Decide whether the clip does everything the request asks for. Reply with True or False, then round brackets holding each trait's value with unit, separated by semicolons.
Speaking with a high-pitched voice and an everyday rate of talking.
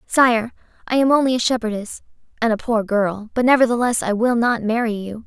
True (230 Hz; 195 wpm)